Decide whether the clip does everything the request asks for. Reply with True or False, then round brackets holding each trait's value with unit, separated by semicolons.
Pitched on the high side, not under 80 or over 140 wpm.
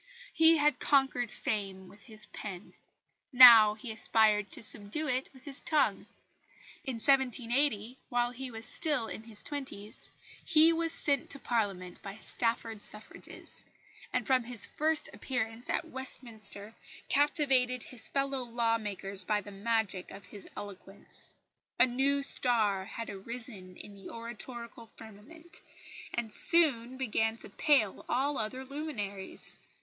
True (235 Hz; 135 wpm)